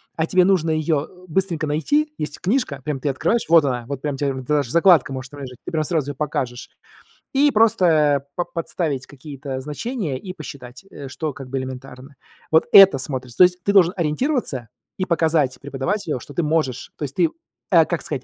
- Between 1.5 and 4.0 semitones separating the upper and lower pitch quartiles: No, average, 4.7 semitones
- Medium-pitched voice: Yes, medium, 150 Hz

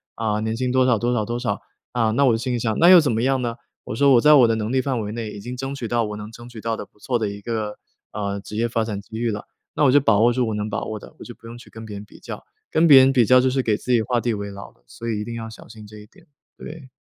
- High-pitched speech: No, low, 115 Hz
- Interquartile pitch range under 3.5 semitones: Yes, average, 2.8 semitones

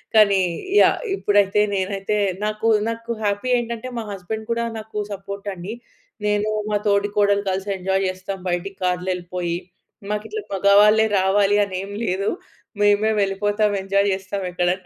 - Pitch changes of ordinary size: No, narrow, 1.7 semitones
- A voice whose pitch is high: Yes, high, 200 Hz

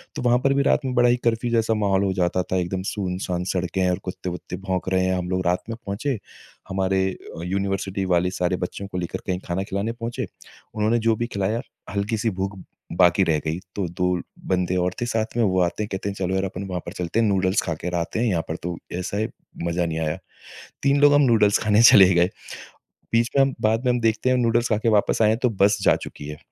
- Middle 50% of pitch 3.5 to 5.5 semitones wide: Yes, average, 3.8 semitones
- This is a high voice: No, very low, 95 Hz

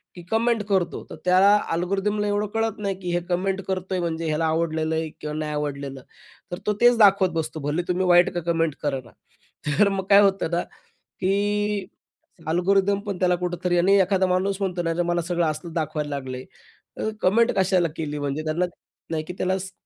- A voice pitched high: No, medium, 180 Hz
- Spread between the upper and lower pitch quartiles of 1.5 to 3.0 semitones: No, average, 3.4 semitones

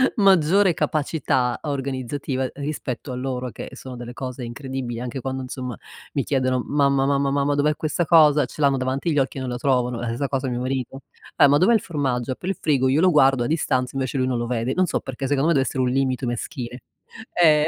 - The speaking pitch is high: No, low, 135 Hz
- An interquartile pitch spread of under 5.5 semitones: Yes, narrow, 2.4 semitones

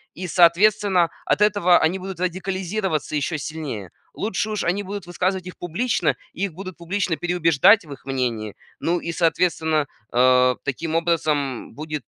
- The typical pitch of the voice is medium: Yes, medium, 170 Hz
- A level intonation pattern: No, average, 3.6 semitones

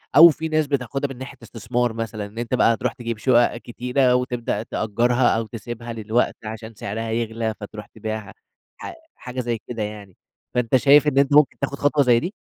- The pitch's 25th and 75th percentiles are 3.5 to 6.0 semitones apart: No, average, 2.8 semitones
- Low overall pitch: Yes, low, 120 Hz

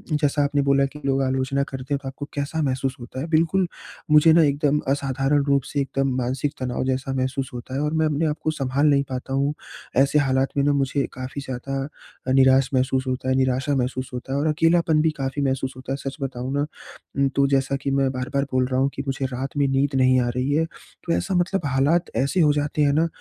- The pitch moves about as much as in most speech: No, narrow, 1.7 semitones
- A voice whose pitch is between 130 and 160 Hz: Yes, low, 135 Hz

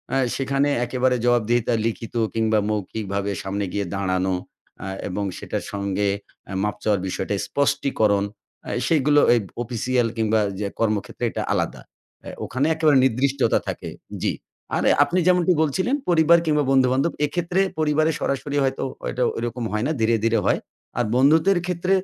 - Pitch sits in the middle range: No, low, 125 Hz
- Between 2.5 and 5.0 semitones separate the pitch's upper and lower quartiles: No, wide, 5.5 semitones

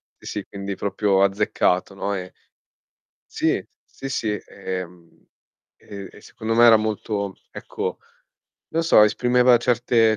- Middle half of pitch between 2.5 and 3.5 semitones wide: Yes, average, 2.8 semitones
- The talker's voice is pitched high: No, low, 105 Hz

